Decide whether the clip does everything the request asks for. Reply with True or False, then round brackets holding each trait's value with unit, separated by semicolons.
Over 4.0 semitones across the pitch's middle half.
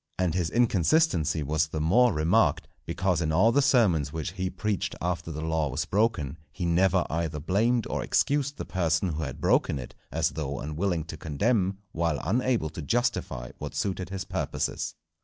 True (5.1 semitones)